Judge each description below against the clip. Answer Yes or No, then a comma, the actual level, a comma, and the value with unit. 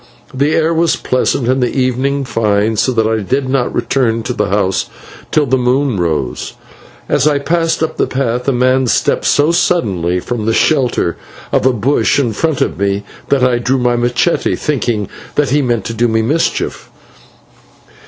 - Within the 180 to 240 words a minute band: Yes, average, 185 wpm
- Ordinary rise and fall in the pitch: Yes, average, 3.8 semitones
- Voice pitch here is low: Yes, low, 125 Hz